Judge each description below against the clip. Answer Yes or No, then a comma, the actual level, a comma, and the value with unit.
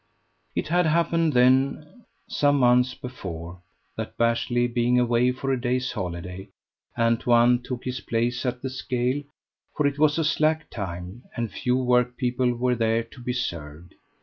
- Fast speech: No, average, 150 wpm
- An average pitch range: No, narrow, 2.0 semitones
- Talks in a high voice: No, low, 125 Hz